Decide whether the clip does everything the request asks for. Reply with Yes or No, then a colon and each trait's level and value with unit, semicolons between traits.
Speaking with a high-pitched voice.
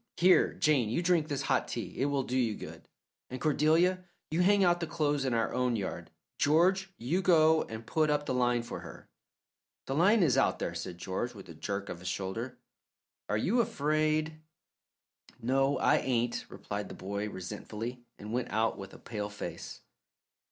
No: low, 130 Hz